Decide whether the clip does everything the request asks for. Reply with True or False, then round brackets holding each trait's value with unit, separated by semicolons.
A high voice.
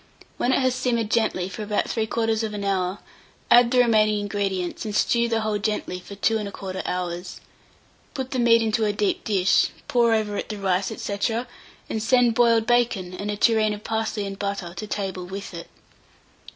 True (215 Hz)